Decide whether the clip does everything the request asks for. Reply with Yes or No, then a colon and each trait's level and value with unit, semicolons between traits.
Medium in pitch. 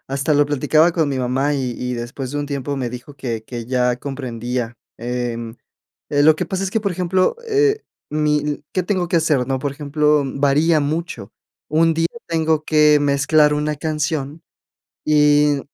Yes: medium, 145 Hz